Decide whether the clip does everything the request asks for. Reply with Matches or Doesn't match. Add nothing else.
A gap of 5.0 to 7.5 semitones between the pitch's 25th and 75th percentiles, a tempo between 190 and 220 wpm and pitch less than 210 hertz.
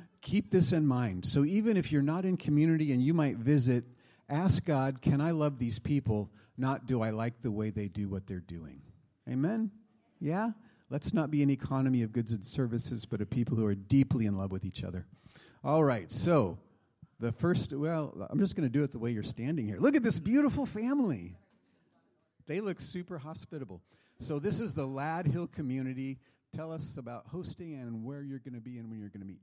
Matches